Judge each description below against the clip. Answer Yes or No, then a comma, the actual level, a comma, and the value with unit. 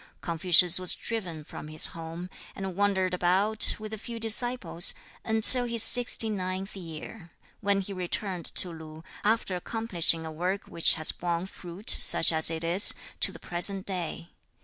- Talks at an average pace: Yes, average, 160 wpm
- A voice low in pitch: No, medium, 185 Hz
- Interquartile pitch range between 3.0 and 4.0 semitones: Yes, average, 3.6 semitones